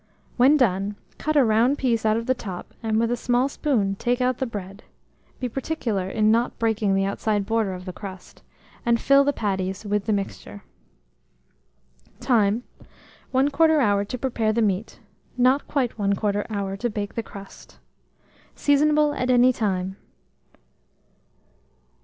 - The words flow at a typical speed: Yes, average, 150 wpm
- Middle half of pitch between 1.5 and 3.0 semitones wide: No, average, 4.1 semitones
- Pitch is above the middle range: Yes, high, 225 Hz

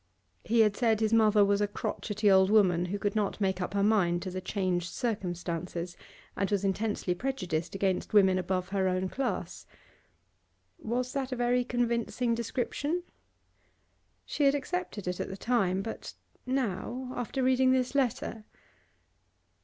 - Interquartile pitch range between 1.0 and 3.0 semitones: No, average, 4.6 semitones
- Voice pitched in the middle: No, high, 210 Hz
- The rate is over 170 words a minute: No, average, 155 wpm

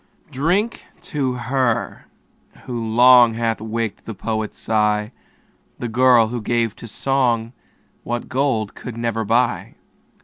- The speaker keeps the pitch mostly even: Yes, narrow, 2.2 semitones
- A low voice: Yes, low, 115 Hz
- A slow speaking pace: Yes, slow, 125 wpm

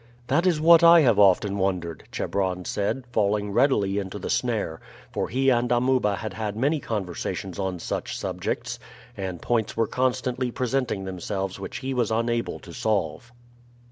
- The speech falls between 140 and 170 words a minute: Yes, average, 160 wpm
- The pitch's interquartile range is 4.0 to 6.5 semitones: Yes, average, 4.7 semitones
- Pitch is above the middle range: No, low, 110 Hz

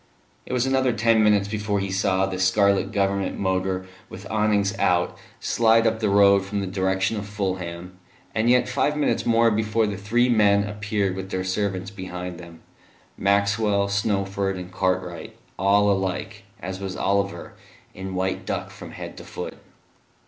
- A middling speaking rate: Yes, average, 165 wpm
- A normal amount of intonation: No, narrow, 2.0 semitones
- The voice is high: No, low, 100 Hz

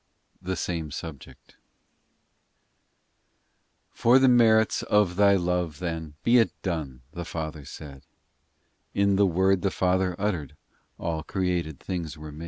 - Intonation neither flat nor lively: Yes, average, 3.7 semitones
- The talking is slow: Yes, slow, 130 wpm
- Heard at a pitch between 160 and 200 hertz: No, very low, 90 Hz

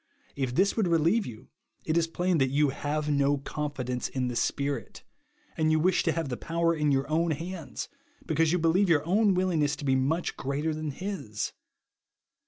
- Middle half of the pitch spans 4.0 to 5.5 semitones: No, average, 3.3 semitones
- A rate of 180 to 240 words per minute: Yes, average, 190 wpm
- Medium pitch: Yes, medium, 155 Hz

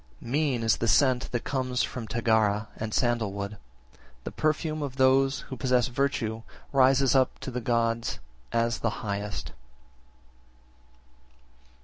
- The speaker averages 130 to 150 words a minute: Yes, slow, 135 wpm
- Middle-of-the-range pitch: No, low, 120 Hz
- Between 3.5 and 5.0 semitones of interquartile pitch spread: No, average, 3.0 semitones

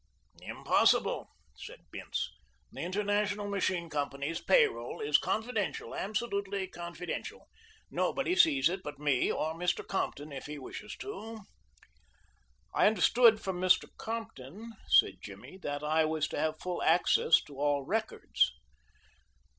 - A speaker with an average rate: No, slow, 130 wpm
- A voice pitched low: No, medium, 185 Hz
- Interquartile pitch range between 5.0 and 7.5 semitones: Yes, wide, 5.6 semitones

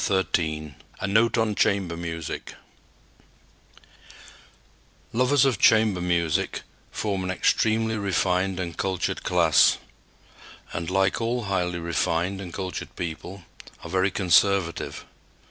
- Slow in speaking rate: Yes, slow, 110 wpm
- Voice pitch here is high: No, very low, 95 Hz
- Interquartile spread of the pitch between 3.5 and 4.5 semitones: No, average, 2.9 semitones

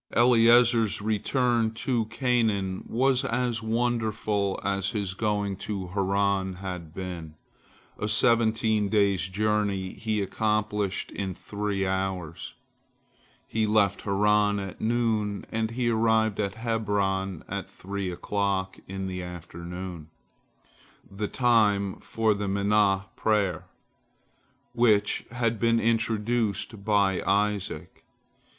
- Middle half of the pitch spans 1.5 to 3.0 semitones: Yes, narrow, 2.5 semitones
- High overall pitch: No, low, 105 Hz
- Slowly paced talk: Yes, slow, 105 wpm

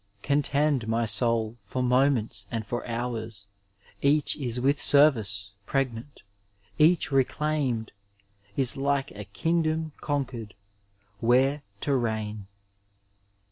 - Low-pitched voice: Yes, low, 125 Hz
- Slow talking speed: Yes, slow, 100 wpm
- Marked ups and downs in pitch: No, average, 4.1 semitones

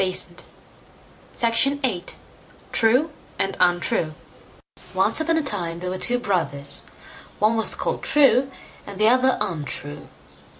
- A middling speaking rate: No, slow, 130 wpm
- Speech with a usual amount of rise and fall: No, wide, 6.5 semitones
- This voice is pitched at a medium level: No, high, 215 Hz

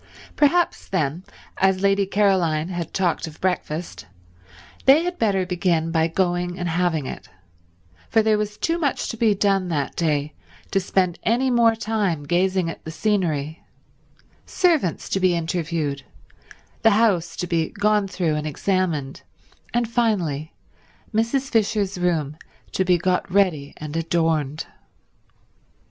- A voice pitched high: No, medium, 180 Hz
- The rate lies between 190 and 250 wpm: No, slow, 135 wpm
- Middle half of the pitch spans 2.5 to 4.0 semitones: No, average, 4.4 semitones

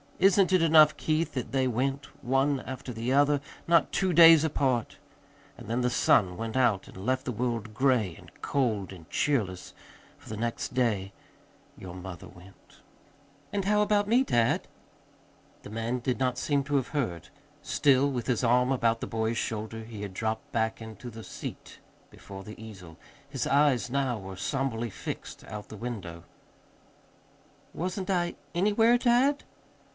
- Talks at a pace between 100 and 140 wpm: No, average, 160 wpm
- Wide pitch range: No, average, 4.7 semitones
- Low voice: Yes, low, 125 Hz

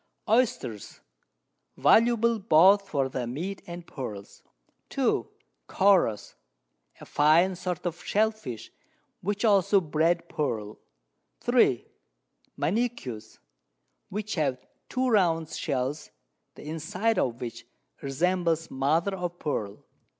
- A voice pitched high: No, medium, 170 Hz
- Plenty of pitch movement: Yes, wide, 6.6 semitones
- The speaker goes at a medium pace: No, slow, 105 wpm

